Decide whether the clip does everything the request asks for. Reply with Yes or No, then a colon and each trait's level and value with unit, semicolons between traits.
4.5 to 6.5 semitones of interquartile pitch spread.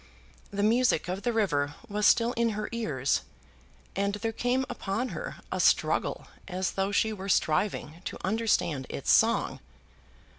No: average, 3.9 semitones